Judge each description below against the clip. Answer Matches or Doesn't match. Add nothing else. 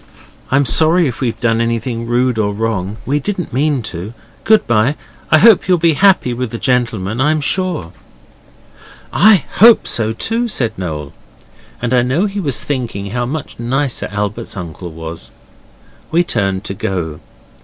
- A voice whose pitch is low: Matches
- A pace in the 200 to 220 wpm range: Doesn't match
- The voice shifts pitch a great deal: Matches